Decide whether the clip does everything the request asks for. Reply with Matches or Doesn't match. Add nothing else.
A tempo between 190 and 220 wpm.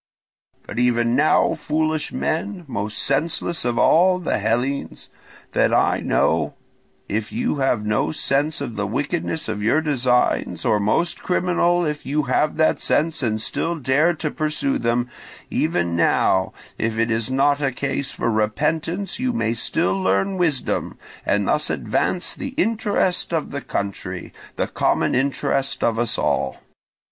Doesn't match